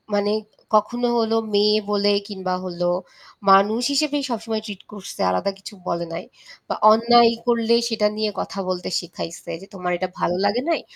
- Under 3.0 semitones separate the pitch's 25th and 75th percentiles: No, average, 3.4 semitones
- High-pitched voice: Yes, high, 210 Hz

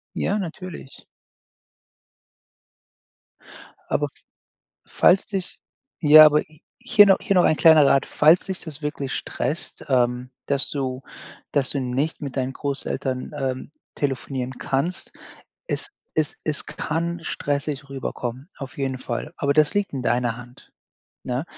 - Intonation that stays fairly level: No, average, 3.3 semitones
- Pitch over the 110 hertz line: Yes, medium, 140 Hz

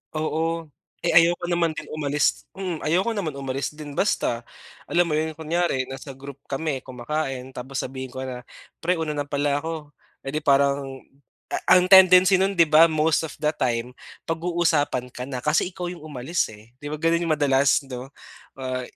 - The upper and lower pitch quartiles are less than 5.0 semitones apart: Yes, average, 3.7 semitones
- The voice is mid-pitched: Yes, medium, 150 Hz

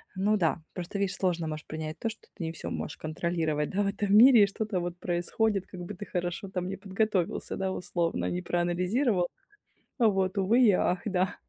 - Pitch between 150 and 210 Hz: Yes, medium, 185 Hz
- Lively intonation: No, average, 2.8 semitones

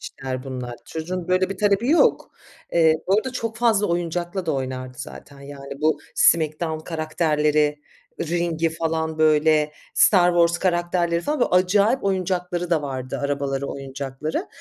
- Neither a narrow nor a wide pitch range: Yes, average, 3.8 semitones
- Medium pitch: Yes, medium, 165 Hz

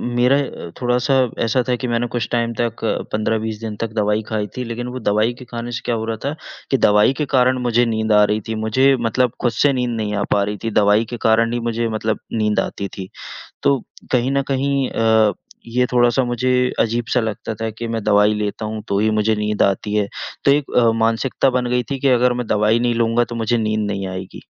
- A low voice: Yes, low, 115 Hz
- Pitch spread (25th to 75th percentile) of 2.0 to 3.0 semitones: Yes, narrow, 2.4 semitones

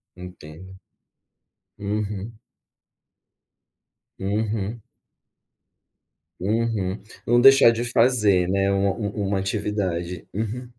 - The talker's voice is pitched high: No, low, 100 Hz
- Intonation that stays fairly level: No, average, 3.1 semitones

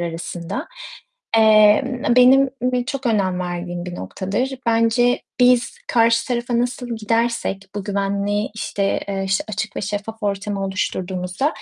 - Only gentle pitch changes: No, average, 3.7 semitones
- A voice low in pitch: No, high, 210 Hz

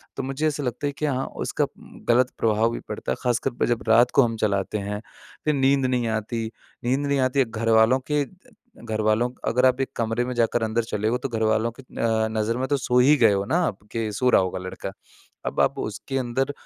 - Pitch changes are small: No, average, 3.0 semitones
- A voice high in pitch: No, low, 120 Hz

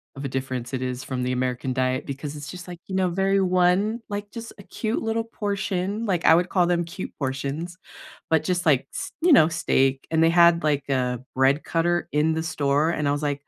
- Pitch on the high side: No, medium, 160 Hz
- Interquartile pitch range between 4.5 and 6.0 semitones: Yes, average, 5.2 semitones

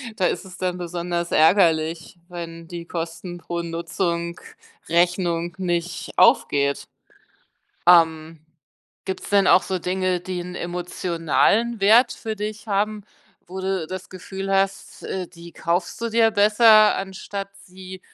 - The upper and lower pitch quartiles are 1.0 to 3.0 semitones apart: Yes, narrow, 2.4 semitones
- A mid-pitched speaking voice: Yes, medium, 180 Hz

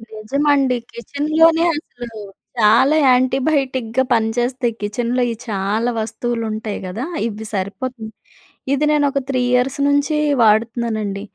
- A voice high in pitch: Yes, high, 245 Hz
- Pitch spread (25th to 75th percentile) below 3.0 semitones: No, average, 3.7 semitones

